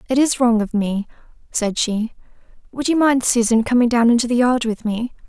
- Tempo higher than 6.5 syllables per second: No, 5.3 syllables/s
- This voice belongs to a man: No, female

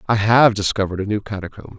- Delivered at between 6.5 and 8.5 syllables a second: Yes, 6.8 syllables/s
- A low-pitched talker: Yes, low, 105 Hz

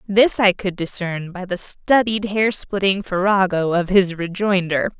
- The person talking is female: Yes, female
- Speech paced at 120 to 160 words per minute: Yes, average, 155 wpm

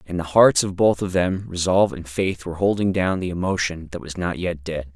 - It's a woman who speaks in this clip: No, male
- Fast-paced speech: Yes, fast, 240 wpm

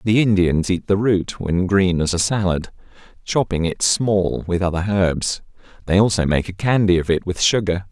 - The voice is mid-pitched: No, very low, 95 Hz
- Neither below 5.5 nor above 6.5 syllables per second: No, 4.7 syllables/s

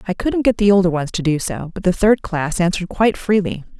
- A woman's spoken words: Yes, female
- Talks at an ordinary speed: No, fast, 255 wpm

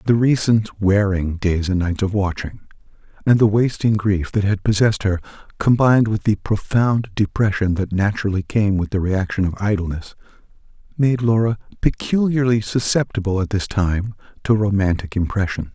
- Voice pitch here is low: Yes, low, 100 Hz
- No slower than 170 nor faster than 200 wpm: No, average, 150 wpm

